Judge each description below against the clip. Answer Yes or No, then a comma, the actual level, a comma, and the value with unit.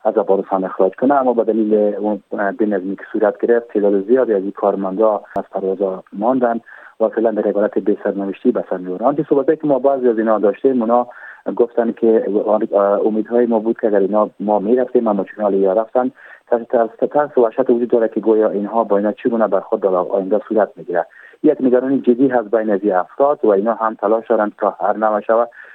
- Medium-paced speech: No, fast, 195 wpm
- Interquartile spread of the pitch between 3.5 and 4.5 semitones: No, average, 3.1 semitones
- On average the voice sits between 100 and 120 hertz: Yes, low, 110 Hz